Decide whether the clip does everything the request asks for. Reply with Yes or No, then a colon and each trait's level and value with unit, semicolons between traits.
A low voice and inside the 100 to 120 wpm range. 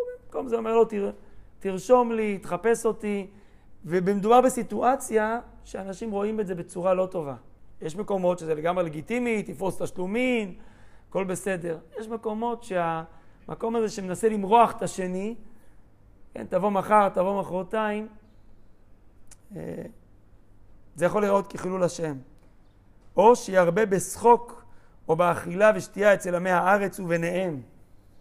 No: medium, 185 Hz; average, 115 wpm